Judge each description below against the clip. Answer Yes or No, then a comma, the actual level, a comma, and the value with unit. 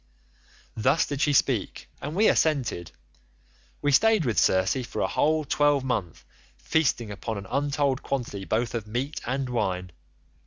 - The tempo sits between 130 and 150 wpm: Yes, average, 145 wpm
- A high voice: No, low, 130 Hz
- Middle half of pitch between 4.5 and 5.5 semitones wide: Yes, average, 5.1 semitones